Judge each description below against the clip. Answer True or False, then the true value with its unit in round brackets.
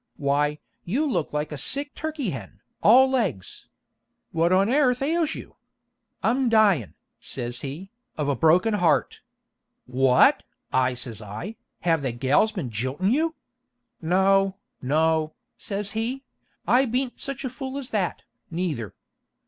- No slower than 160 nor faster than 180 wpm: False (140 wpm)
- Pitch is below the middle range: False (185 Hz)